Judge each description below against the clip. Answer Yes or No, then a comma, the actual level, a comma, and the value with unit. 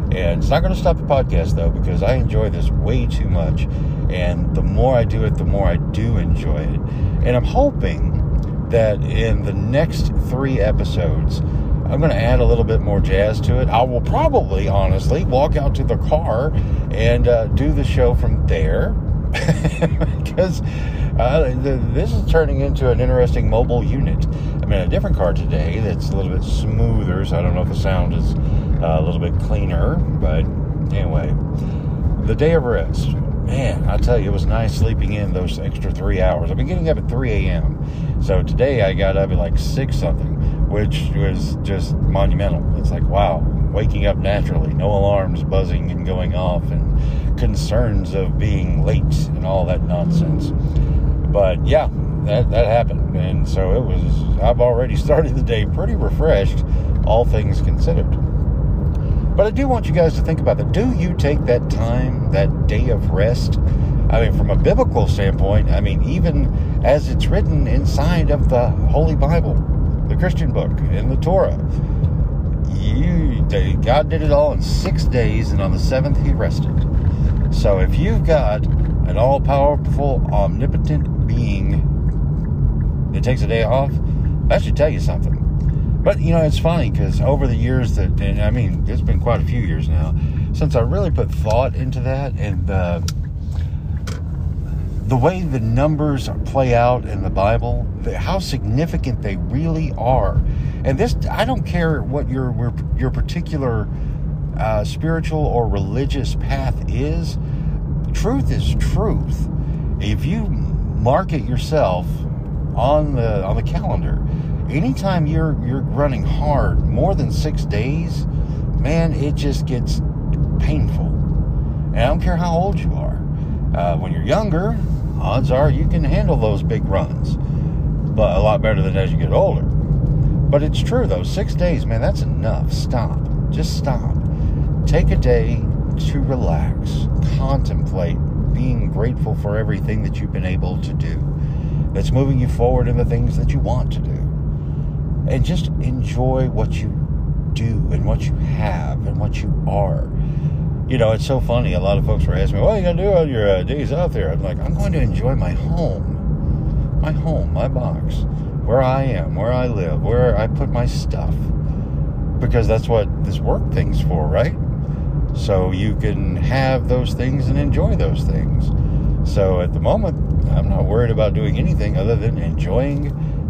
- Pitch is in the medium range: No, low, 100 Hz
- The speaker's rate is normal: Yes, average, 175 wpm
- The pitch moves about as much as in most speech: No, wide, 8.4 semitones